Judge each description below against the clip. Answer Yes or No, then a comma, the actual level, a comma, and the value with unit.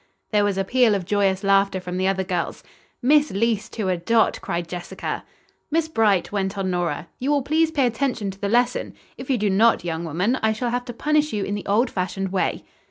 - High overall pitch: Yes, high, 205 Hz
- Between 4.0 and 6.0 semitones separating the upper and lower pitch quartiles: Yes, average, 4.5 semitones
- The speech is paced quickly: Yes, fast, 225 wpm